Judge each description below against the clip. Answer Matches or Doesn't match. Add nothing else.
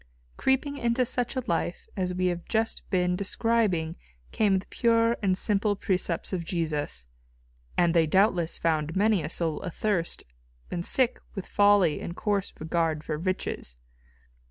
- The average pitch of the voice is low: Doesn't match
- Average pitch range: Matches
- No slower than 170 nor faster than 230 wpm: Doesn't match